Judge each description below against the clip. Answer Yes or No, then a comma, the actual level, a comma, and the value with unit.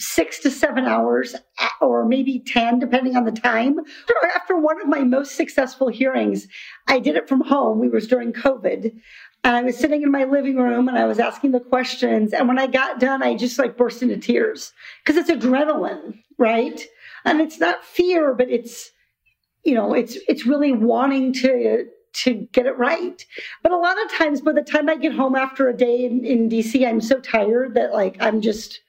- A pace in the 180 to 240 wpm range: Yes, average, 200 wpm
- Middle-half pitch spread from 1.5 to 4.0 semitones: Yes, average, 3.2 semitones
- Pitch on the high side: Yes, very high, 260 Hz